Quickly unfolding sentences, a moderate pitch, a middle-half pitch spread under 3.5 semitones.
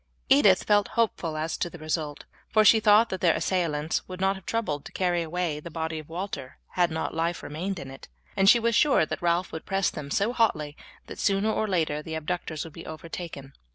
No: fast, 220 wpm; medium, 170 Hz; average, 3.8 semitones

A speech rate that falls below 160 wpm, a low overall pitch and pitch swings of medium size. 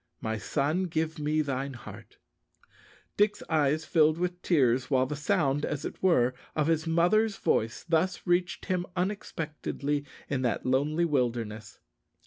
No: average, 140 wpm; medium, 150 Hz; average, 4.6 semitones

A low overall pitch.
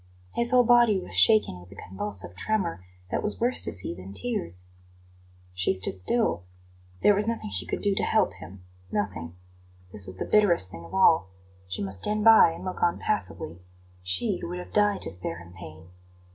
Yes: low, 100 Hz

